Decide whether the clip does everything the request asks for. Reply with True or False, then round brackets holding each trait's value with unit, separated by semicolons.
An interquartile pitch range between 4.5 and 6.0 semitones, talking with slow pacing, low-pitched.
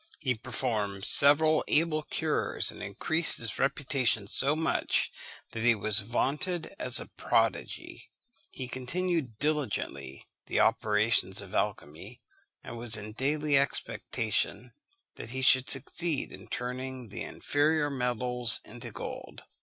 True (5.0 semitones; 125 wpm; 125 Hz)